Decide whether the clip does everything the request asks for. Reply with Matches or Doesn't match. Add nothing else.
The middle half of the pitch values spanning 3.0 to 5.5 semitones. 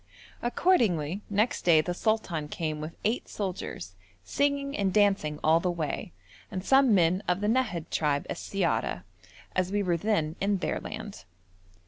Matches